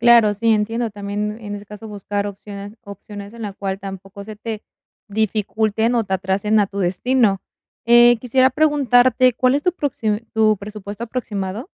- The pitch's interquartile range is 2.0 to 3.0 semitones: Yes, average, 2.7 semitones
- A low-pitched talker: No, high, 210 Hz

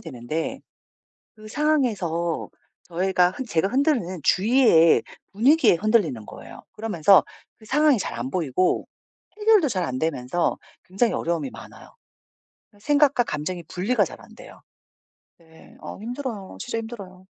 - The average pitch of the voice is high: Yes, high, 195 Hz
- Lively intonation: Yes, wide, 6.6 semitones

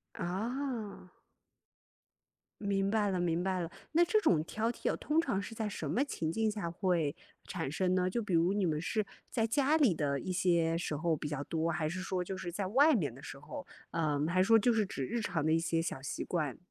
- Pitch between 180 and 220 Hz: Yes, medium, 185 Hz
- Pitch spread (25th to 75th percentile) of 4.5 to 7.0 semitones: Yes, average, 5.0 semitones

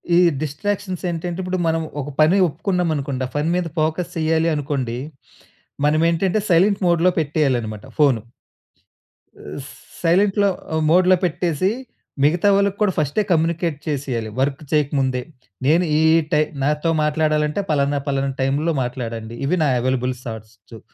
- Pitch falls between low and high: Yes, medium, 155 Hz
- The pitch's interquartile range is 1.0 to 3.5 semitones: No, average, 4.2 semitones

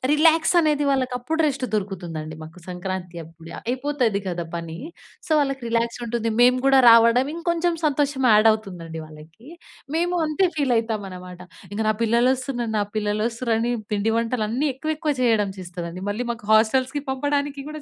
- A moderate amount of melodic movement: No, wide, 5.8 semitones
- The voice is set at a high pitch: Yes, high, 230 Hz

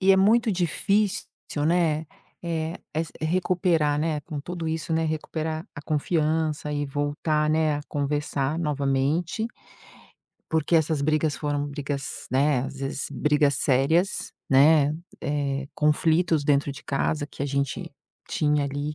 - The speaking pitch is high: No, medium, 150 Hz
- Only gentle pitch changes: Yes, narrow, 2.1 semitones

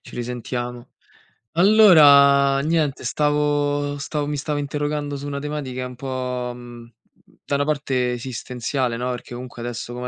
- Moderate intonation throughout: Yes, average, 3.0 semitones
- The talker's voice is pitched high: No, medium, 140 Hz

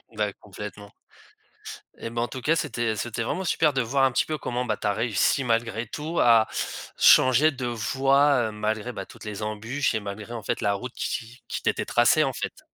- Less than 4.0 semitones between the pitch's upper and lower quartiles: Yes, average, 3.4 semitones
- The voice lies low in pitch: Yes, low, 120 Hz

